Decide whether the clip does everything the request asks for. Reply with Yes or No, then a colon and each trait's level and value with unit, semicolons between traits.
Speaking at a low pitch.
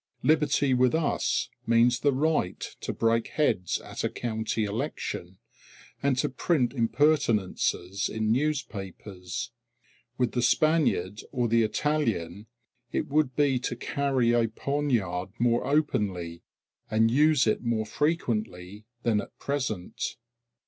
Yes: low, 120 Hz